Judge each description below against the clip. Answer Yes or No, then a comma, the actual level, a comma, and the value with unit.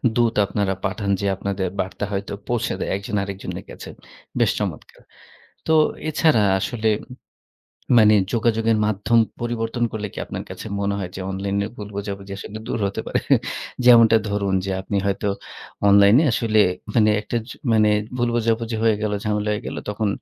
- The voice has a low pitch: Yes, low, 105 Hz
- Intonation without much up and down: Yes, narrow, 2.3 semitones